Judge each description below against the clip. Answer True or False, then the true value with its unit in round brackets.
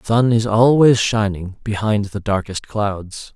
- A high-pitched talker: False (105 Hz)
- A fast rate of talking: False (160 wpm)